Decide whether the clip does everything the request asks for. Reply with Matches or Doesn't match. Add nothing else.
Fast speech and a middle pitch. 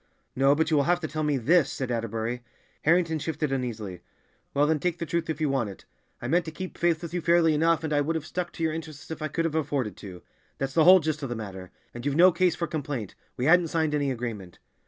Matches